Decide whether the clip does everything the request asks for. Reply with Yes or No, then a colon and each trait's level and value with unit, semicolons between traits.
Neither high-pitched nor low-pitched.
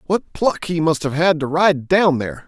Yes: medium, 160 Hz